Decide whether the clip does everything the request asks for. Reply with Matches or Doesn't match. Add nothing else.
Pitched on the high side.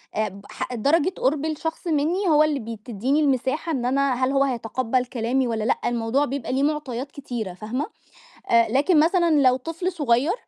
Matches